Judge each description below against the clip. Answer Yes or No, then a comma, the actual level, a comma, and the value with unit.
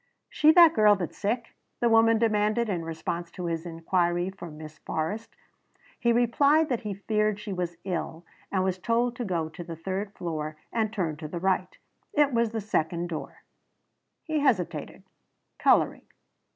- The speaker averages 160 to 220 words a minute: Yes, average, 165 wpm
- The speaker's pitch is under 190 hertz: No, high, 195 Hz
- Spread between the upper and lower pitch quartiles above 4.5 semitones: Yes, average, 5.1 semitones